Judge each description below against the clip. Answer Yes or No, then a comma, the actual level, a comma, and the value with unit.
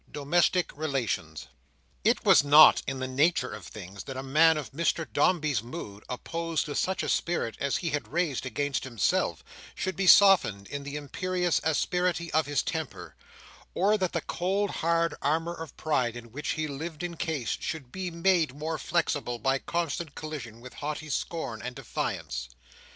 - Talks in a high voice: No, medium, 150 Hz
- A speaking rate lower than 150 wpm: No, average, 165 wpm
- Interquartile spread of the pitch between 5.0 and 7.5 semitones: No, average, 4.3 semitones